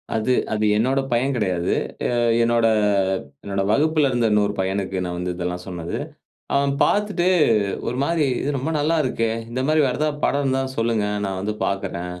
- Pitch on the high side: No, low, 115 Hz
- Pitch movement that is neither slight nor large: No, wide, 6.2 semitones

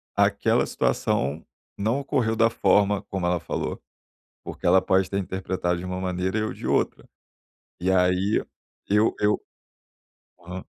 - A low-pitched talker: Yes, very low, 95 Hz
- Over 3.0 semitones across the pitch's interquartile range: No, narrow, 2.4 semitones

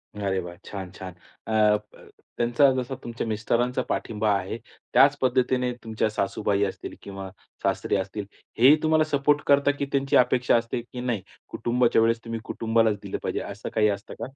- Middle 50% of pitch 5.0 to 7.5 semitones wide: No, average, 3.3 semitones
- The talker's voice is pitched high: No, low, 115 Hz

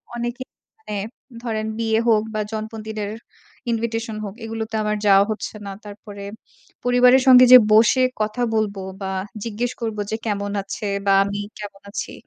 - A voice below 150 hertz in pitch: No, high, 220 Hz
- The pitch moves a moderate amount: No, narrow, 2.0 semitones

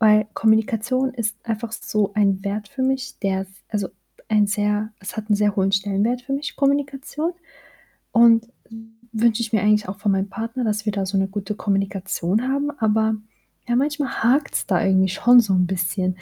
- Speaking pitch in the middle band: No, high, 215 Hz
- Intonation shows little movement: No, average, 3.2 semitones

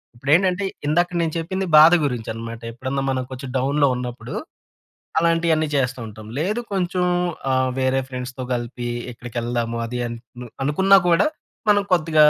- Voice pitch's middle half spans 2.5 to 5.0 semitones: No, wide, 5.4 semitones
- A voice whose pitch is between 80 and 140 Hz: Yes, low, 135 Hz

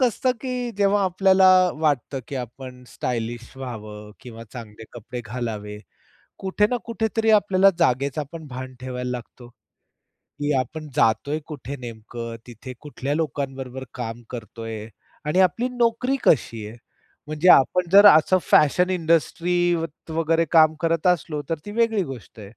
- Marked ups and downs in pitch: Yes, wide, 6.9 semitones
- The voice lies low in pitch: No, medium, 145 Hz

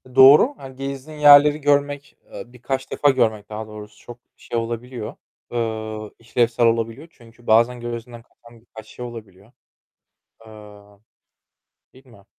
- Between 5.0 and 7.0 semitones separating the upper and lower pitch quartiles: No, average, 3.2 semitones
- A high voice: No, low, 120 Hz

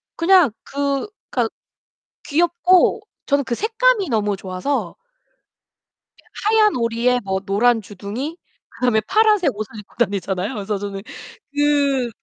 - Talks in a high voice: Yes, very high, 250 Hz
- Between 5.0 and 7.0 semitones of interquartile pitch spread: No, wide, 8.2 semitones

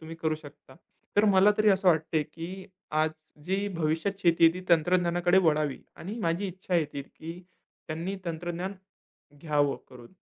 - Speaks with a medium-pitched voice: Yes, medium, 170 Hz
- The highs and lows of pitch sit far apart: No, average, 2.9 semitones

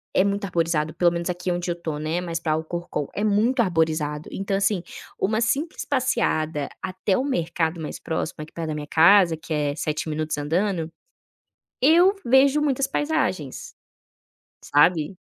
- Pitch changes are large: No, average, 4.6 semitones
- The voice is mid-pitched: Yes, medium, 175 Hz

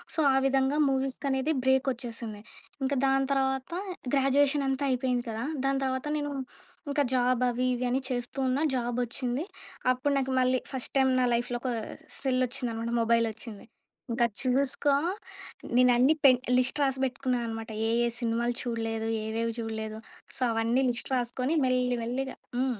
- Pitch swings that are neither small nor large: No, narrow, 2.1 semitones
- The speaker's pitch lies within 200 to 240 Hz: No, very high, 255 Hz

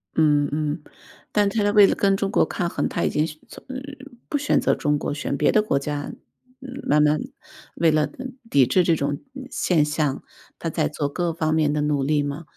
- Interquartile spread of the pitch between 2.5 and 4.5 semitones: Yes, average, 3.3 semitones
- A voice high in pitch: No, medium, 155 Hz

